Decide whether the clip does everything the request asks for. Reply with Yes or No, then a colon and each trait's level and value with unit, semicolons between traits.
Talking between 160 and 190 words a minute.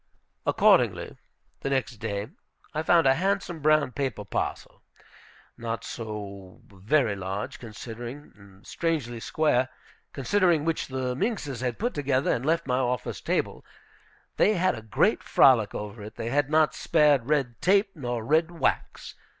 No: average, 150 wpm